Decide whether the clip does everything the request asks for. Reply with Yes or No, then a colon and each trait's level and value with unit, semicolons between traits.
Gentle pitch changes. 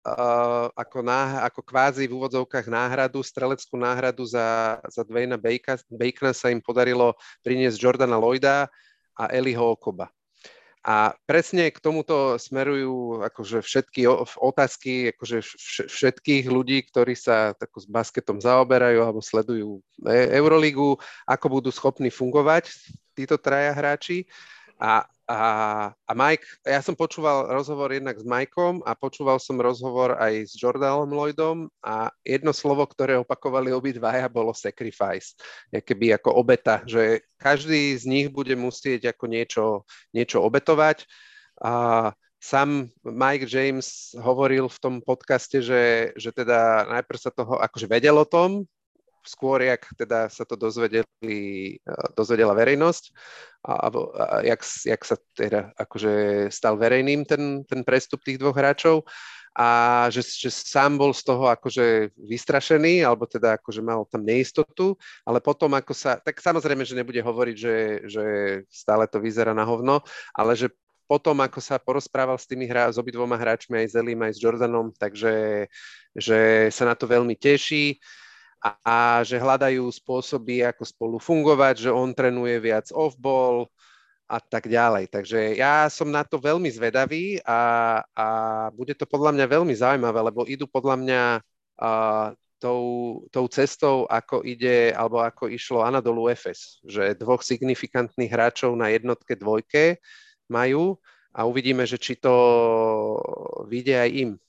No: average, 3.0 semitones